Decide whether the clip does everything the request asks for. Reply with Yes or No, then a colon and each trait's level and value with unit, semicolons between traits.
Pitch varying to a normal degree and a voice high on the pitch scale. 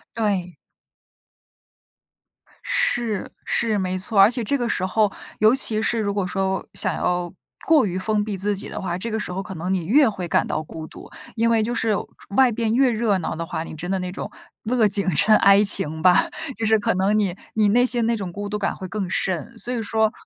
Yes: average, 3.2 semitones; high, 205 Hz